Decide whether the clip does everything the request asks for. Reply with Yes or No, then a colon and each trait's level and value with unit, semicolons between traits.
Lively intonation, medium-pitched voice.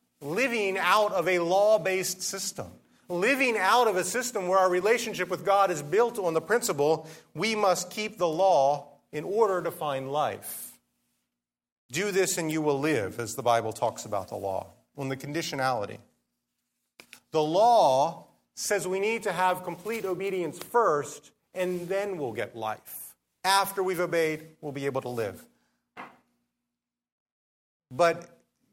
Yes: wide, 6.3 semitones; medium, 175 Hz